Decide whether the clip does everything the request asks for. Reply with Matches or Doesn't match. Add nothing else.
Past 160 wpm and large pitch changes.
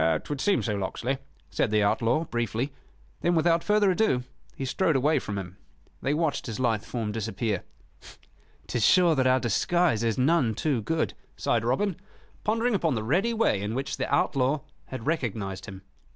Matches